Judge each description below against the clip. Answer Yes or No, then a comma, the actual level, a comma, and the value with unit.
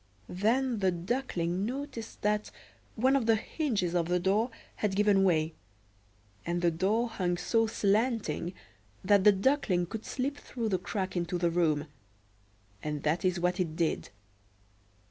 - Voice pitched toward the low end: No, high, 195 Hz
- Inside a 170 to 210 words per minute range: No, average, 150 wpm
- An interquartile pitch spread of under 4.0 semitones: No, average, 4.4 semitones